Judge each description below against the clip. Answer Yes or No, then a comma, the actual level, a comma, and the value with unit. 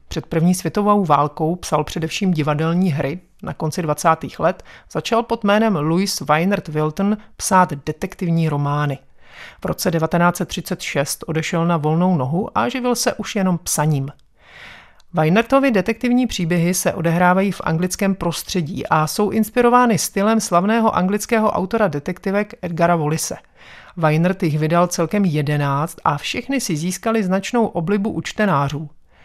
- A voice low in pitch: No, medium, 180 Hz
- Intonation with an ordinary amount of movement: Yes, average, 4.7 semitones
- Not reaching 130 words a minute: No, average, 135 wpm